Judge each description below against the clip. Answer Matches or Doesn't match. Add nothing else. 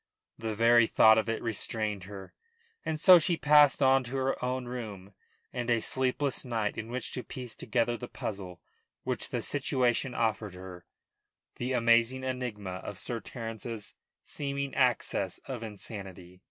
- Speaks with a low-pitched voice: Matches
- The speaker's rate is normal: Matches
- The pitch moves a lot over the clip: Doesn't match